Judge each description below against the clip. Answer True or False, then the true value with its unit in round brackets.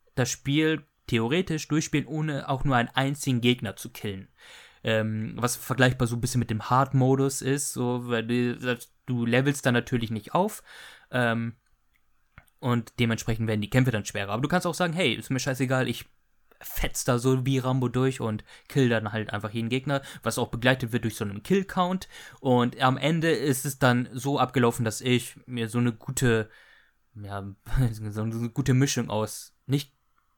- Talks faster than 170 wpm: True (180 wpm)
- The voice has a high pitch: False (125 Hz)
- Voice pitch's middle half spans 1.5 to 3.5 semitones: True (3.0 semitones)